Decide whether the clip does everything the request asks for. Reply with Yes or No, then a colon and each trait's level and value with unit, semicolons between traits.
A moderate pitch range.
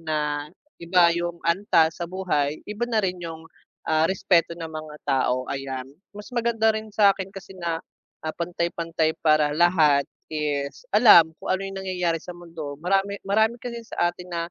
Yes: average, 3.6 semitones